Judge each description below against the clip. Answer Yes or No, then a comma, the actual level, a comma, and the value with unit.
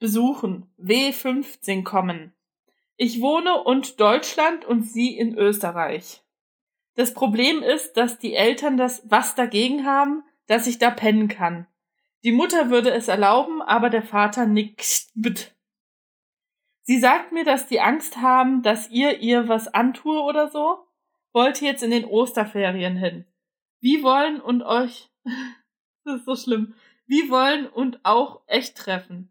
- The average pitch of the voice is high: Yes, high, 245 Hz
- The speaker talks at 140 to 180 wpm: Yes, average, 145 wpm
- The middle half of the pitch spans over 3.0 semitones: Yes, average, 4.0 semitones